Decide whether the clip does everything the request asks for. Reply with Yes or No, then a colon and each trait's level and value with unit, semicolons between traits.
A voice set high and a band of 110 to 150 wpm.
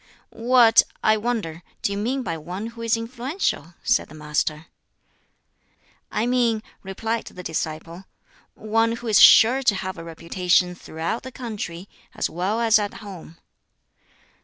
Yes: high, 210 Hz; average, 145 wpm